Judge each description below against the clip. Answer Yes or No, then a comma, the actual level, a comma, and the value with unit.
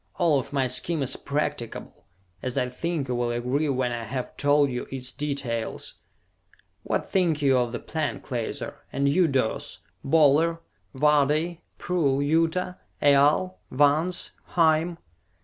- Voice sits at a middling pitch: Yes, medium, 145 Hz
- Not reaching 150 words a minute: Yes, average, 140 wpm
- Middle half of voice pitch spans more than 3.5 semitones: Yes, average, 4.0 semitones